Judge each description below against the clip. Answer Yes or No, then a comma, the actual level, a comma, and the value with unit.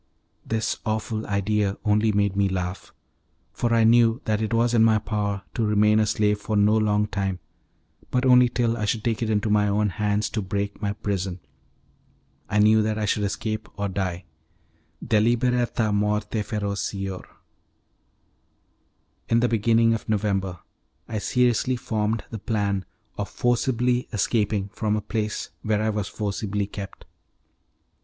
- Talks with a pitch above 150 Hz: No, low, 105 Hz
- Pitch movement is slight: Yes, narrow, 1.7 semitones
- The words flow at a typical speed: Yes, average, 150 wpm